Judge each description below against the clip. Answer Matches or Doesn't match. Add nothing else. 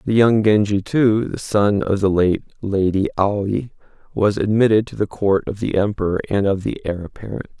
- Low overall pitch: Matches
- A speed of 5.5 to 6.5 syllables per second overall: Doesn't match